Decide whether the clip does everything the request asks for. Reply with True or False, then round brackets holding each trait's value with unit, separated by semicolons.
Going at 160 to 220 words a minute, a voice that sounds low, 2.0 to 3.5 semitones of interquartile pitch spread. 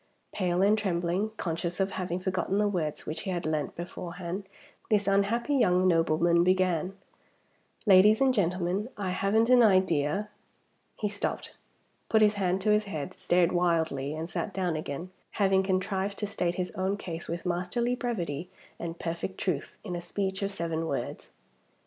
False (165 wpm; 185 Hz; 2.8 semitones)